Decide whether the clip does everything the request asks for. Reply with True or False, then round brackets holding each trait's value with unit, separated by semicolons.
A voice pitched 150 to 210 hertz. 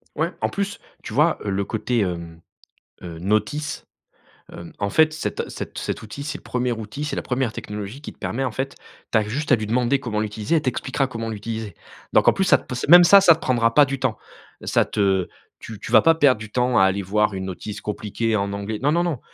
False (115 Hz)